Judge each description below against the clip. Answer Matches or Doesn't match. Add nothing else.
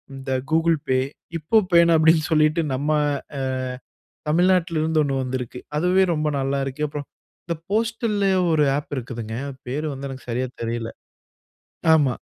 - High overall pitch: Doesn't match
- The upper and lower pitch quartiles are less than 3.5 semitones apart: Doesn't match